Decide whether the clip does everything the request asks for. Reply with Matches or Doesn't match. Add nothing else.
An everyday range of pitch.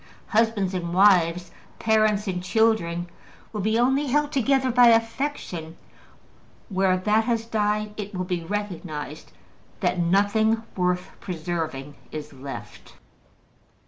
Matches